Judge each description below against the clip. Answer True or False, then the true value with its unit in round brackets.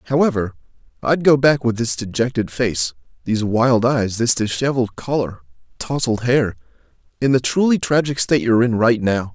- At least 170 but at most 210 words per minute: False (155 wpm)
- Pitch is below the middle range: True (120 Hz)